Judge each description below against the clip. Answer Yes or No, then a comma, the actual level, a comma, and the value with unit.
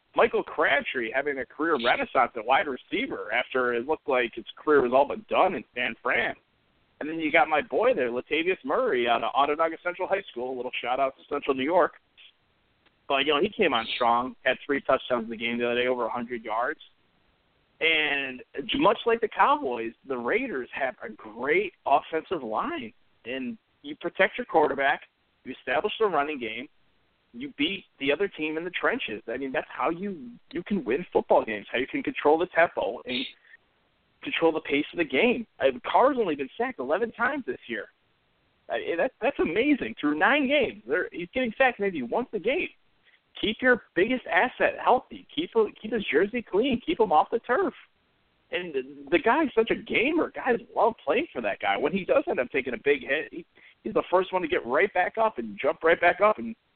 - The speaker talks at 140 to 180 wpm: No, fast, 205 wpm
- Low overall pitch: No, high, 200 Hz